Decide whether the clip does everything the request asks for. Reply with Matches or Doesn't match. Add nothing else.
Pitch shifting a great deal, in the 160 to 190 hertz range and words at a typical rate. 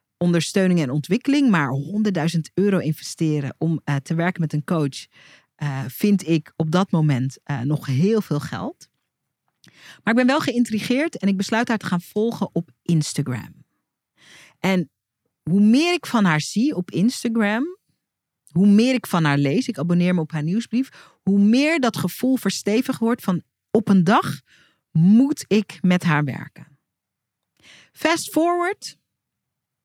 Matches